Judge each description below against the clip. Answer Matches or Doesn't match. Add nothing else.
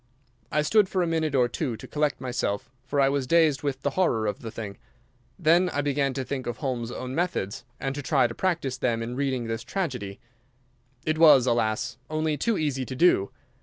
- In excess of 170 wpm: Matches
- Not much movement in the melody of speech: Doesn't match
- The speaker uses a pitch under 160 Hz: Matches